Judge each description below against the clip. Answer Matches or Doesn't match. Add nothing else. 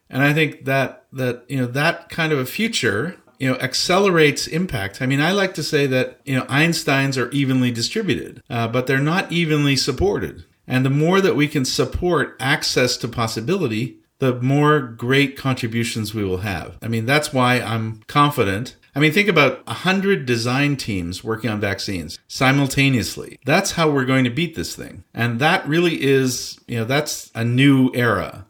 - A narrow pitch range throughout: Doesn't match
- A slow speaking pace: Doesn't match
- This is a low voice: Matches